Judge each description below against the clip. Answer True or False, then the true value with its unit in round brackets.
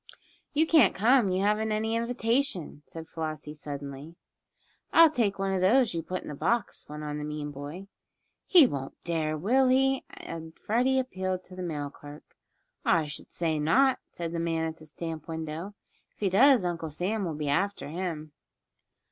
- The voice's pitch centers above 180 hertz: False (175 Hz)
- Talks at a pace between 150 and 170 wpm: False (180 wpm)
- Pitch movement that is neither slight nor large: False (6.2 semitones)